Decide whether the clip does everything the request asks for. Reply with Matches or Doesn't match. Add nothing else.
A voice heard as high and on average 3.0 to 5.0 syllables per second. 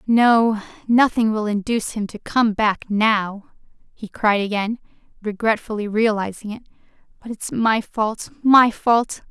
Matches